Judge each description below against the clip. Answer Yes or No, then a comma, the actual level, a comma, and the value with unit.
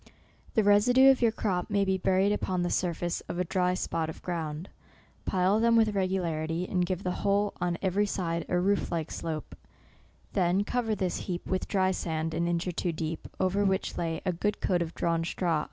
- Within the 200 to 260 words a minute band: Yes, fast, 205 wpm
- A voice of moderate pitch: Yes, medium, 180 Hz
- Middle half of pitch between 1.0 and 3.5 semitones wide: Yes, average, 2.8 semitones